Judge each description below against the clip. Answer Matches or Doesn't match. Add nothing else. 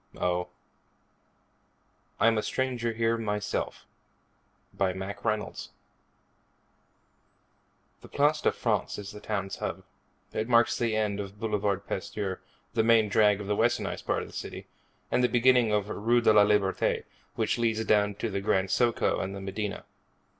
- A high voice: Doesn't match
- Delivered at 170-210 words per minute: Doesn't match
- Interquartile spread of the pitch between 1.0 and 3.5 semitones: Matches